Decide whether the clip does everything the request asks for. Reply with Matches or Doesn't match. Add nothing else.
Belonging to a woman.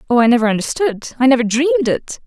Matches